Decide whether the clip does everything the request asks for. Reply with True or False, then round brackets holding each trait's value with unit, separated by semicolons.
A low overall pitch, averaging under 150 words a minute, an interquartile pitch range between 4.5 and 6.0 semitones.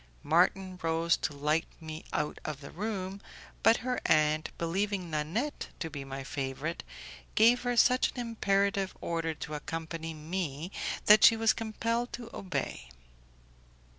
False (170 Hz; 140 wpm; 5.6 semitones)